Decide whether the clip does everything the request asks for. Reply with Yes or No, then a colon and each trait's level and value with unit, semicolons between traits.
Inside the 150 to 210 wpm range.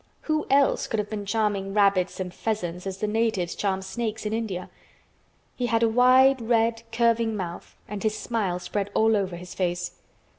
Yes: average, 180 wpm